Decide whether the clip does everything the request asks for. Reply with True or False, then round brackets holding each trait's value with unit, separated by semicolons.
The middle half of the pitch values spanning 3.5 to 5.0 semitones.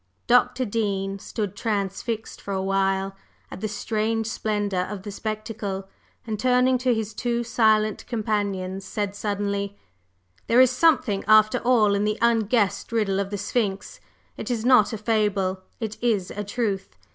False (2.4 semitones)